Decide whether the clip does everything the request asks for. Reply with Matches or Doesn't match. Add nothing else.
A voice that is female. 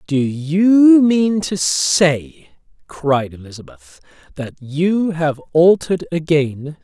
Doesn't match